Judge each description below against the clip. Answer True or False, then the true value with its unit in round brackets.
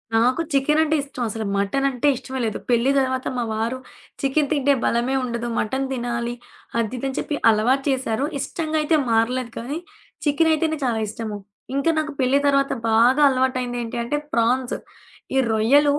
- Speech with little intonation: False (3.0 semitones)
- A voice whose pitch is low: False (260 Hz)